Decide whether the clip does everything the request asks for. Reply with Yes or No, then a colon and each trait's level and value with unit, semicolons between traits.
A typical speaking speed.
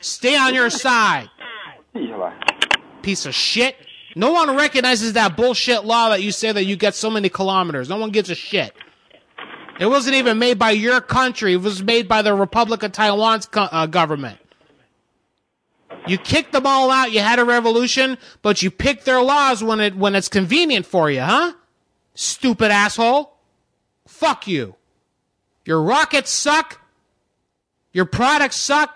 Yes: average, 160 wpm